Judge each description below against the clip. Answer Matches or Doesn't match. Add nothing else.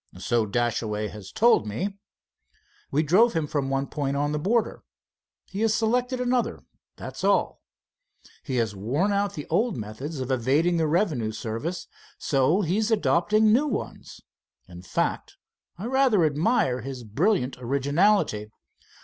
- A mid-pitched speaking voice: Matches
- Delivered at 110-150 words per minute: Matches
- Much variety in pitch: Matches